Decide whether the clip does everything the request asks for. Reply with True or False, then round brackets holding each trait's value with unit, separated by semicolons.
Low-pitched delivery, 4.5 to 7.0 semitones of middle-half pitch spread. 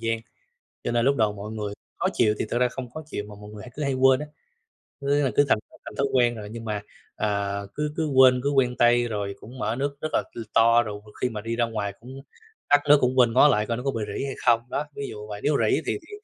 False (120 Hz; 3.9 semitones)